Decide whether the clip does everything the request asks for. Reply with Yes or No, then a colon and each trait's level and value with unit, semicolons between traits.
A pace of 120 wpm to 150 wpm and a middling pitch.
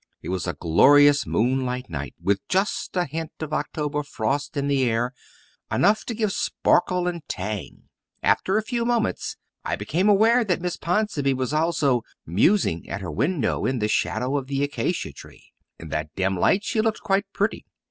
No: average, 180 wpm; medium, 145 Hz